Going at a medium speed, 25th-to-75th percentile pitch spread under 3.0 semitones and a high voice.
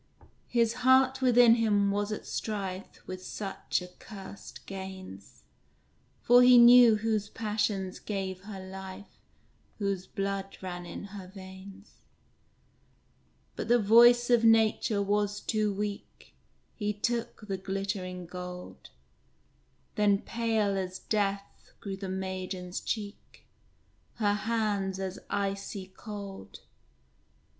No: slow, 110 wpm; narrow, 2.4 semitones; high, 200 Hz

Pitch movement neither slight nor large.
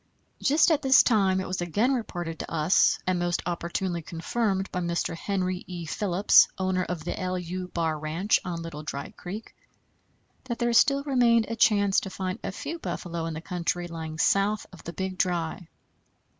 Yes: average, 3.3 semitones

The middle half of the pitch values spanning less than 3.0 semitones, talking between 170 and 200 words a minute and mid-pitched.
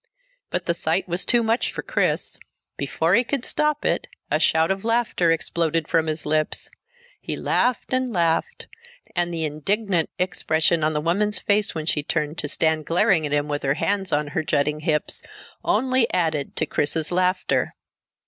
No: average, 4.7 semitones; average, 175 wpm; medium, 165 Hz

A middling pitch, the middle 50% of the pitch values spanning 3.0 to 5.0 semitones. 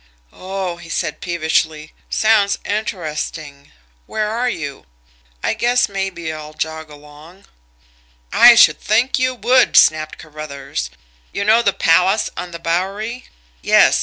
No: medium, 175 Hz; wide, 5.5 semitones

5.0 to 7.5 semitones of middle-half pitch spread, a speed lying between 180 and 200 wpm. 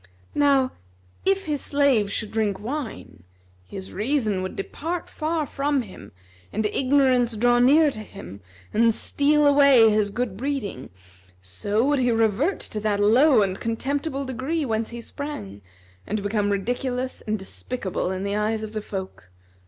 No: wide, 5.4 semitones; average, 150 wpm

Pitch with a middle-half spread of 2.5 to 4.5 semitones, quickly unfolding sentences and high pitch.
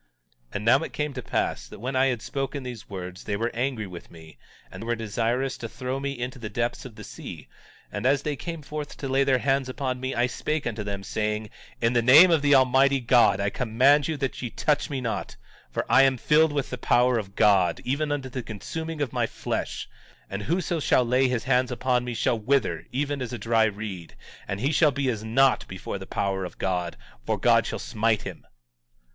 No: average, 3.9 semitones; fast, 225 wpm; low, 125 Hz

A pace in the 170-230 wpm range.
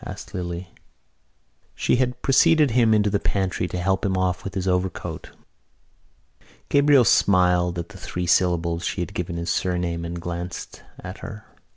No: average, 160 wpm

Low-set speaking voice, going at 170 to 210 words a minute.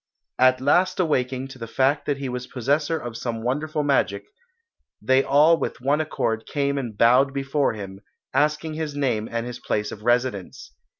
Yes: low, 130 Hz; average, 175 wpm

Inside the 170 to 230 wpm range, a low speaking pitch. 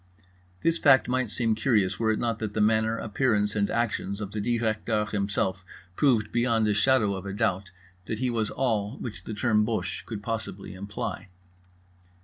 Yes: average, 175 wpm; low, 110 Hz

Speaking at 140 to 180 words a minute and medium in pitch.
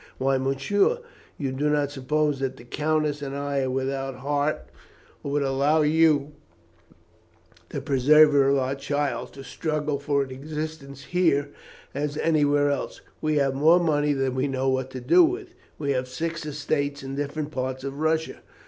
Yes: average, 165 wpm; medium, 145 Hz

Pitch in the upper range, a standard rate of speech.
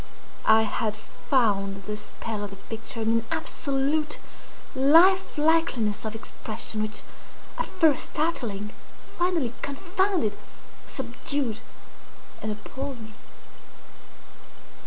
No: high, 230 Hz; slow, 100 wpm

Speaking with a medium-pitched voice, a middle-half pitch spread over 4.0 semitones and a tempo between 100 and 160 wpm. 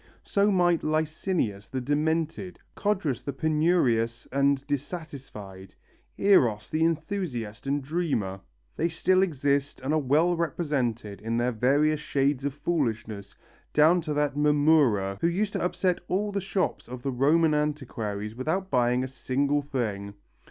Yes: medium, 145 Hz; average, 5.0 semitones; average, 140 wpm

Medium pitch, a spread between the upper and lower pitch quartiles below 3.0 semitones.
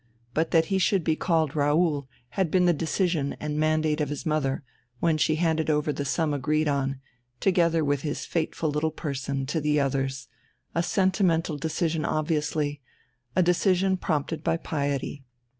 Yes: medium, 155 Hz; narrow, 2.5 semitones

